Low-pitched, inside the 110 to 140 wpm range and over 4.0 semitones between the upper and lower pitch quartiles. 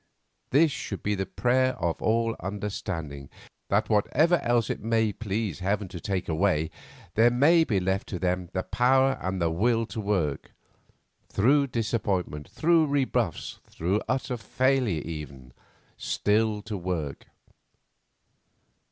Yes: low, 105 Hz; slow, 135 wpm; average, 5.0 semitones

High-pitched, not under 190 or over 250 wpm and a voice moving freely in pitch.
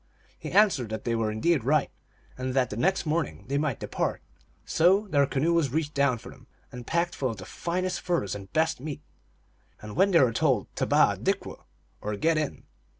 No: medium, 140 Hz; average, 200 wpm; wide, 6.3 semitones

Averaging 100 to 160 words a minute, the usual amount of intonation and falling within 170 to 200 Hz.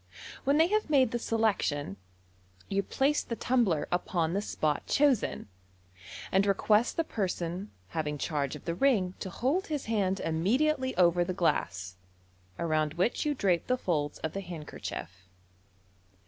No: average, 155 wpm; wide, 7.6 semitones; high, 190 Hz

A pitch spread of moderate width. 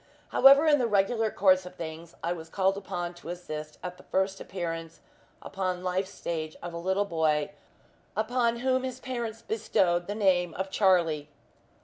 Yes: average, 3.9 semitones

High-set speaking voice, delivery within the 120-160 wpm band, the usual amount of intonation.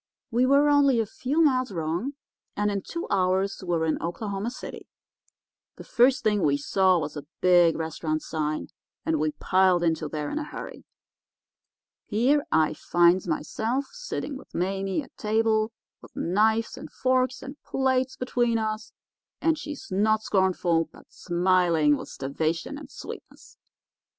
No: high, 200 Hz; average, 150 wpm; wide, 7.2 semitones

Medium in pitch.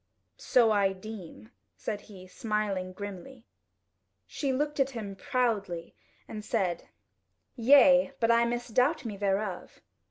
No: high, 215 Hz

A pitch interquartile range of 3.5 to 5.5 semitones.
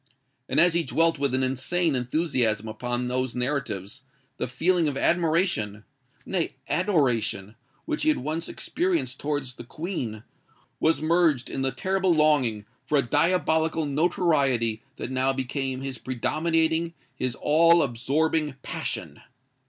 Yes: average, 4.7 semitones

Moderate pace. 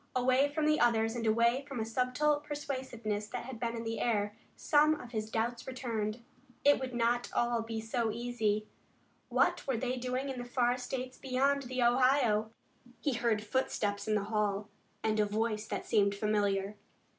Yes: average, 180 wpm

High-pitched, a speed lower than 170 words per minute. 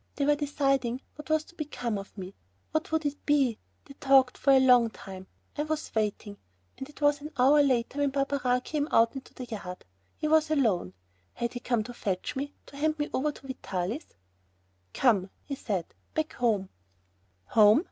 No: very high, 265 Hz; average, 190 wpm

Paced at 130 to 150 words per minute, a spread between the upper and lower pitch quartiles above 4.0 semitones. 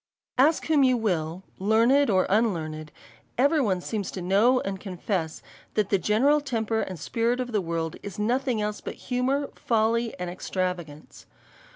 No: average, 160 wpm; average, 5.2 semitones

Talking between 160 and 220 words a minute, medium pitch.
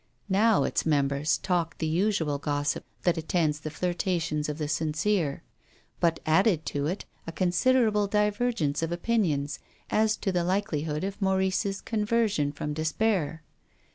No: average, 140 wpm; medium, 170 Hz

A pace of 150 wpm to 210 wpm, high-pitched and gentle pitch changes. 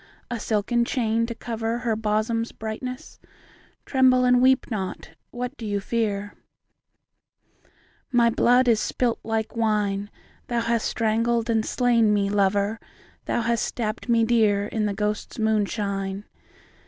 No: average, 140 wpm; high, 225 Hz; narrow, 2.2 semitones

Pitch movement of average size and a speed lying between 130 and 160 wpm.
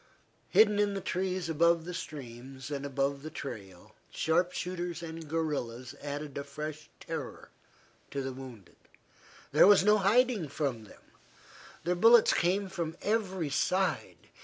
Yes: average, 5.0 semitones; average, 140 wpm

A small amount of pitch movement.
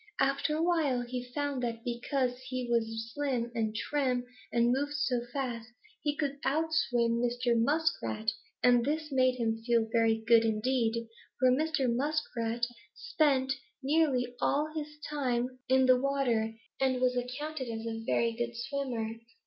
No: average, 3.2 semitones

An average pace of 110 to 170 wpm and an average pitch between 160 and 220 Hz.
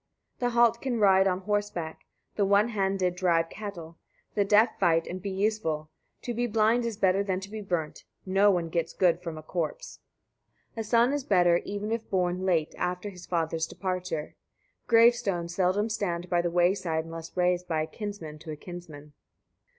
No: average, 190 wpm; medium, 185 Hz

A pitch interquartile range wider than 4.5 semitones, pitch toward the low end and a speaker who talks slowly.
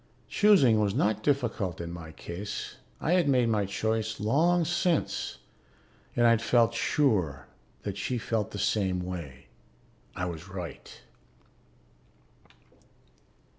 Yes: average, 5.3 semitones; low, 110 Hz; slow, 120 wpm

